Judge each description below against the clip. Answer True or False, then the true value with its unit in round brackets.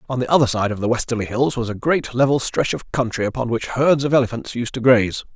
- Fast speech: True (260 wpm)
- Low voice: True (120 Hz)